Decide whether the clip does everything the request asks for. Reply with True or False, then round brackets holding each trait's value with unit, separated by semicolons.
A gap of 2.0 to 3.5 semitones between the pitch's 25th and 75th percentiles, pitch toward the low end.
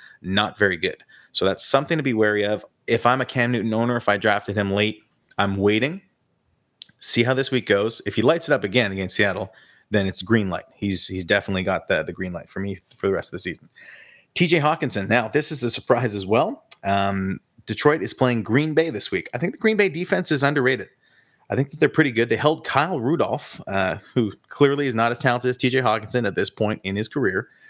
False (5.2 semitones; 115 Hz)